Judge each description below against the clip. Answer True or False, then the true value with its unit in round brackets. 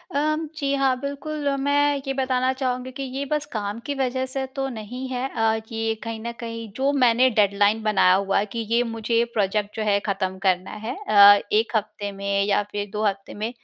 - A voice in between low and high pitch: False (230 Hz)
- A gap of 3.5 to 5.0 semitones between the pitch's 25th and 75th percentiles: True (4.2 semitones)